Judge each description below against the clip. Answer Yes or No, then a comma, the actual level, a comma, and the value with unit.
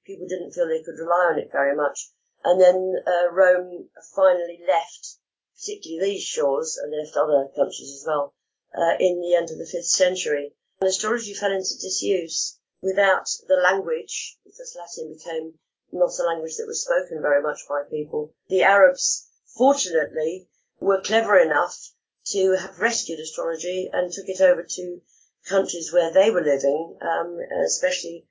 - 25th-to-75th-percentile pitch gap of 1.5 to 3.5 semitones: No, average, 5.0 semitones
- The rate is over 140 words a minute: Yes, average, 160 wpm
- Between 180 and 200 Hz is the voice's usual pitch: Yes, medium, 185 Hz